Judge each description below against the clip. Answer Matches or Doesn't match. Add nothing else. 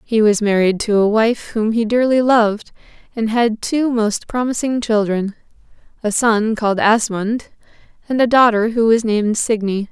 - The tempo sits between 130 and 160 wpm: Matches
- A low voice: Doesn't match